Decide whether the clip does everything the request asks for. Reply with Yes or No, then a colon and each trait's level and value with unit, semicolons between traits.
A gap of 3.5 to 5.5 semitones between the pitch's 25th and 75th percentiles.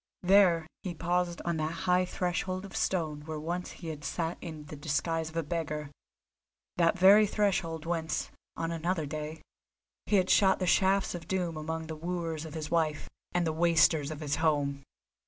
No: narrow, 2.4 semitones